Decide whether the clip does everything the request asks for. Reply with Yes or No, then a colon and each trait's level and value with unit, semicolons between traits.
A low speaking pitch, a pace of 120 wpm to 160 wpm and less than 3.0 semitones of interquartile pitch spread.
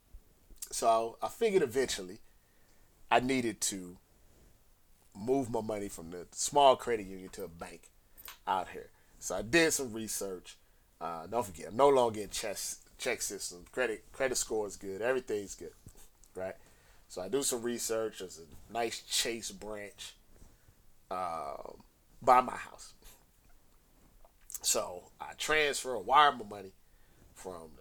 No: low, 105 Hz; average, 140 wpm; average, 4.1 semitones